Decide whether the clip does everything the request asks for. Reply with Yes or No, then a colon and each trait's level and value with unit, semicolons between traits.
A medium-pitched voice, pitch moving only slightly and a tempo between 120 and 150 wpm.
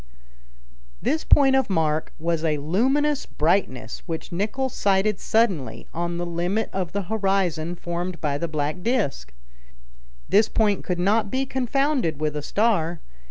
No: medium, 180 Hz; wide, 5.5 semitones; average, 145 wpm